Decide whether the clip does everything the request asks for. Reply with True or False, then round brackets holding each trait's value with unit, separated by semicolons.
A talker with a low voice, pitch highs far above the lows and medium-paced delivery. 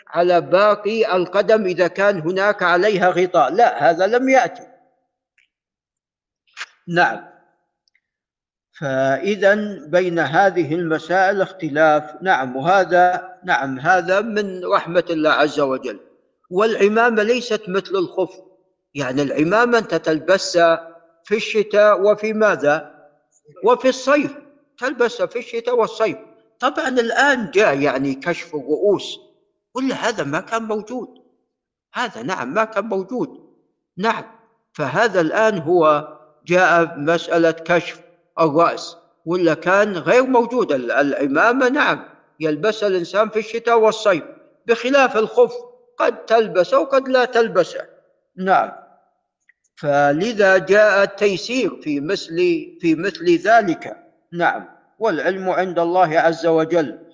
False (200 Hz; 6.0 semitones; 105 wpm)